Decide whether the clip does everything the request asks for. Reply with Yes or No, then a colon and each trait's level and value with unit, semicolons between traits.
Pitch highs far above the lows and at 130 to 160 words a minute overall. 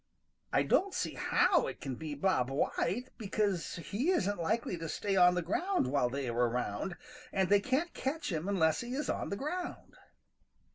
No: wide, 8.1 semitones; average, 185 wpm